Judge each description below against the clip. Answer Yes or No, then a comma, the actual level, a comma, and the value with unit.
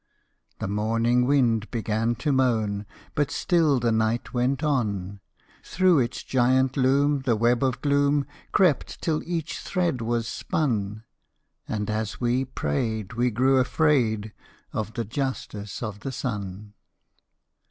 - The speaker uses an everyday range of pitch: Yes, average, 3.9 semitones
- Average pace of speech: No, slow, 130 wpm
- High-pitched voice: No, low, 120 Hz